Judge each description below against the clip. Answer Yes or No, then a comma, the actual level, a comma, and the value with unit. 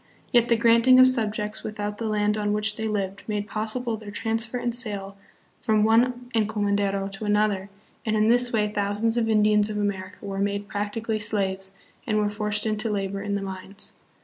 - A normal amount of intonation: No, narrow, 1.7 semitones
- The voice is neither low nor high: No, high, 210 Hz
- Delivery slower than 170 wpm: No, average, 190 wpm